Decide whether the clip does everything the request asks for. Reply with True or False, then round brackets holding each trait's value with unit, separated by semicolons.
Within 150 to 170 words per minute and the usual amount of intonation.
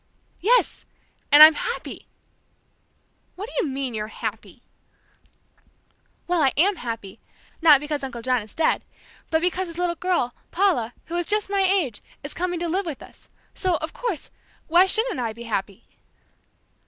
False (160 wpm; 6.5 semitones)